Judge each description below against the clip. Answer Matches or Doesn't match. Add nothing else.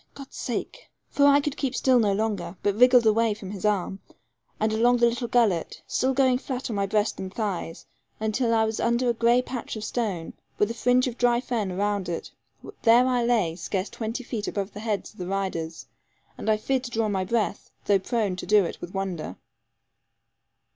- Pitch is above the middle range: Matches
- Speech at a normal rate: Doesn't match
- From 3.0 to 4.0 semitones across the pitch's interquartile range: Matches